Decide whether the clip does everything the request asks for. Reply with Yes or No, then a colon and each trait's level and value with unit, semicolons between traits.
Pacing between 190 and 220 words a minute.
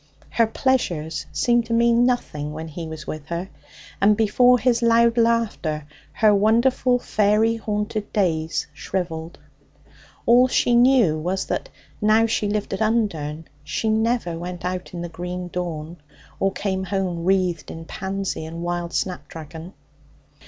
No: average, 145 wpm